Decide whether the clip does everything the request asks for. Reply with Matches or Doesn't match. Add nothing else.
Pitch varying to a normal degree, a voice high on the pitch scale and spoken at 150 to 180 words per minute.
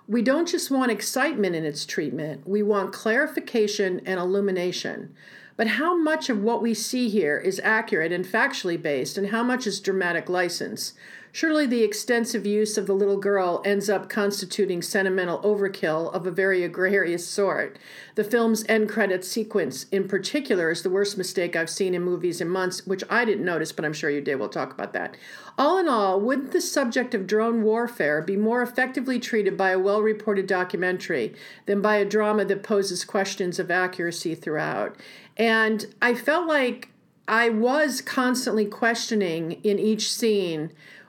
Matches